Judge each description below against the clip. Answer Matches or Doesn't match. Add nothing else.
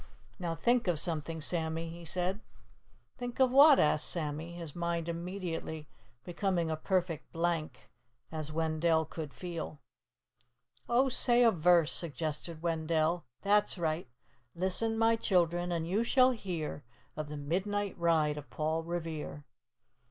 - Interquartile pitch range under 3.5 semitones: Matches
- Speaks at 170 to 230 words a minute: Doesn't match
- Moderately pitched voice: Matches